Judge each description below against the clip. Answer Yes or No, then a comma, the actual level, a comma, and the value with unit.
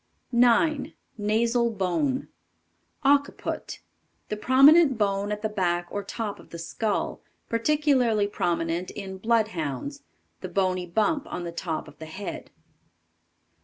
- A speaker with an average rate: No, slow, 125 wpm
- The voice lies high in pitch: Yes, high, 210 Hz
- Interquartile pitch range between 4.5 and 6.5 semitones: Yes, average, 5.3 semitones